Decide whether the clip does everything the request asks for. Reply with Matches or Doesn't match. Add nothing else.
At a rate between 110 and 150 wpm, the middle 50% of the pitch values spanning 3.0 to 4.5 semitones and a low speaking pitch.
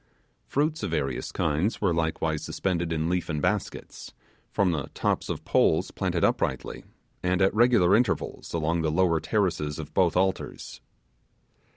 Matches